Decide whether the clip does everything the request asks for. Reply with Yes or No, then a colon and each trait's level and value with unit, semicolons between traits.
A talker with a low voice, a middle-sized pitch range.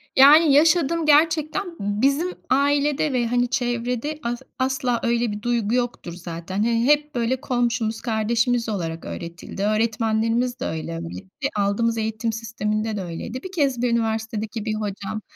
No: high, 235 Hz; average, 3.6 semitones